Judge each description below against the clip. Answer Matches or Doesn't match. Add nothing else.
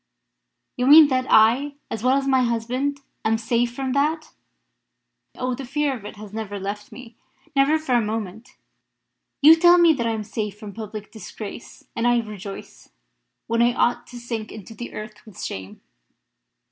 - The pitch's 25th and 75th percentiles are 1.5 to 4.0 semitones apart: Matches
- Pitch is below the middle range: Doesn't match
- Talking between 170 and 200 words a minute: Matches